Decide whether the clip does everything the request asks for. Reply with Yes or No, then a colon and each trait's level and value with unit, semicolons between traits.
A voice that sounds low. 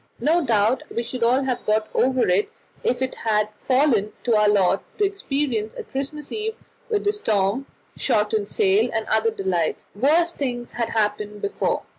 No: high, 230 Hz